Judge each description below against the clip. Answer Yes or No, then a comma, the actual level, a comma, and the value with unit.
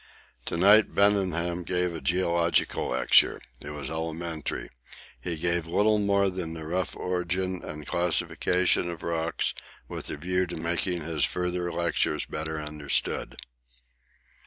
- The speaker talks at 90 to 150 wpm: Yes, slow, 135 wpm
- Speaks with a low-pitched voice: Yes, very low, 85 Hz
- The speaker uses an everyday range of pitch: No, narrow, 2.0 semitones